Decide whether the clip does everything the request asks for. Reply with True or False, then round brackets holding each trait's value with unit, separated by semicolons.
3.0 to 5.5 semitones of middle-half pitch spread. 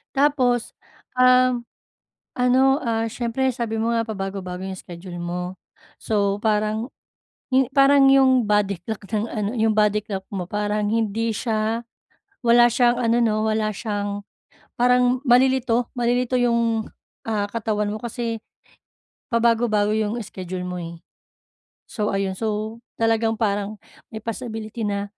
False (2.6 semitones)